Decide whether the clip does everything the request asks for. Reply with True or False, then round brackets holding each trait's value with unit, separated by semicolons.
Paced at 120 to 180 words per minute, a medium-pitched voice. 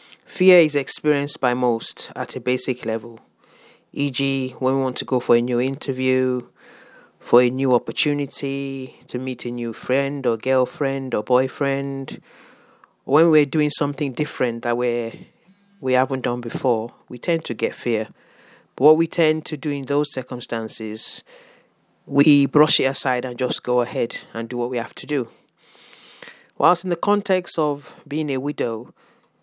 False (165 wpm; 130 Hz)